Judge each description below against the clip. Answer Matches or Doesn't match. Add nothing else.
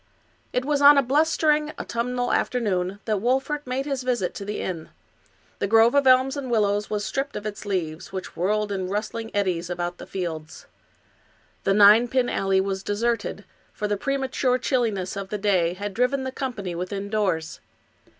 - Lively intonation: Doesn't match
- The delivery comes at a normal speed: Matches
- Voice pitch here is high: Matches